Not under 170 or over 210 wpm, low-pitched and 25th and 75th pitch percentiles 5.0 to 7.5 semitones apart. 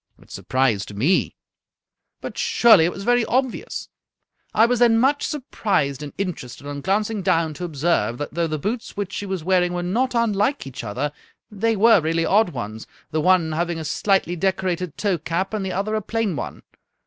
No: average, 195 wpm; medium, 185 Hz; wide, 5.5 semitones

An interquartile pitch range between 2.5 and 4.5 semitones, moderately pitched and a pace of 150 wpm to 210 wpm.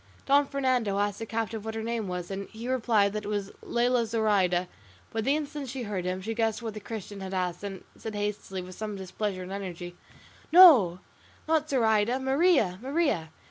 No: average, 4.2 semitones; high, 215 Hz; average, 190 wpm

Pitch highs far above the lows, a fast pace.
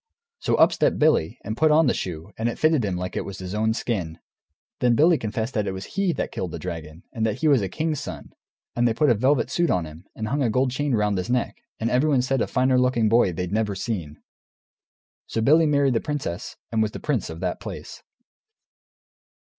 Yes: wide, 5.7 semitones; fast, 225 wpm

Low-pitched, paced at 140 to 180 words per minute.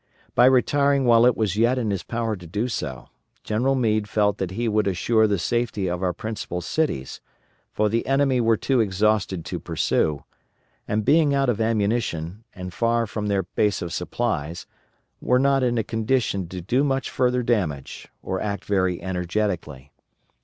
Yes: low, 110 Hz; average, 175 wpm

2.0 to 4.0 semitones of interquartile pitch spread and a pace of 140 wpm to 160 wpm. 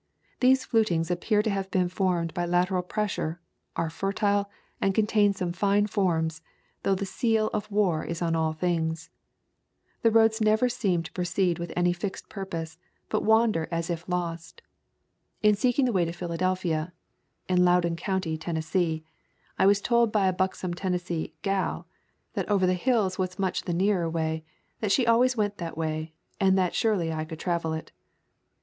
No: average, 3.4 semitones; average, 170 wpm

